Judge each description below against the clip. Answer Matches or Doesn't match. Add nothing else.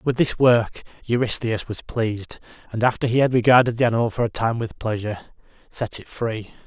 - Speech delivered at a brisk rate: Doesn't match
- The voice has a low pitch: Matches